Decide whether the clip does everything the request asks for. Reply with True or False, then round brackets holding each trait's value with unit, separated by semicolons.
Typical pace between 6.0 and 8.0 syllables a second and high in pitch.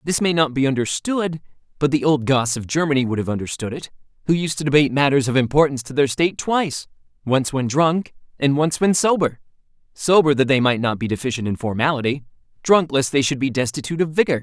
False (6.2 syllables/s; 140 Hz)